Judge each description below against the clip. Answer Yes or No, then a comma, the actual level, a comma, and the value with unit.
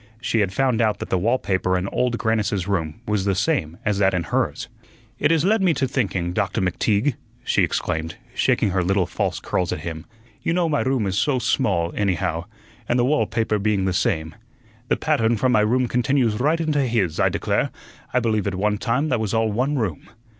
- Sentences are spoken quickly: Yes, fast, 210 wpm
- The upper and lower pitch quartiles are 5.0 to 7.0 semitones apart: Yes, average, 5.3 semitones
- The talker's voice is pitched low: Yes, low, 110 Hz